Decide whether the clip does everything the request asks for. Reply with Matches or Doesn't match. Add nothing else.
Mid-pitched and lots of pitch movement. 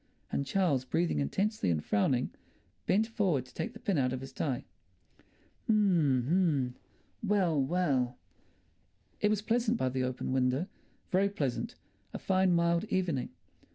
Matches